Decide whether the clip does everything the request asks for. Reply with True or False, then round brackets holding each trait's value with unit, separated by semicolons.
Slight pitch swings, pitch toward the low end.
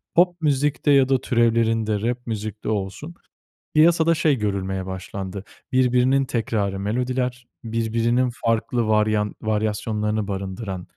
False (3.5 semitones; 115 Hz)